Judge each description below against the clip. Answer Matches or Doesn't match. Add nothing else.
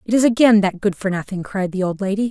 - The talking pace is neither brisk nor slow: Doesn't match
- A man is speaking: Doesn't match